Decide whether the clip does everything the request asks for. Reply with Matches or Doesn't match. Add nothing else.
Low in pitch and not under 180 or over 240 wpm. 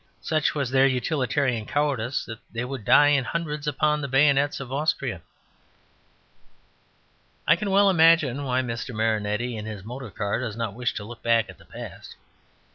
Doesn't match